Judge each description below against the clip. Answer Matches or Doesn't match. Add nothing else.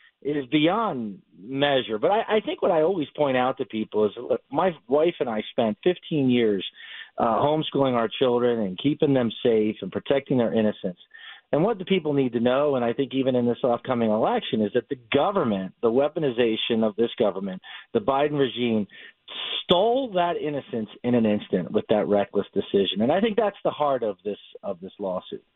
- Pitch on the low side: Matches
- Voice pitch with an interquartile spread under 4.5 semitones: Doesn't match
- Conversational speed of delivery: Matches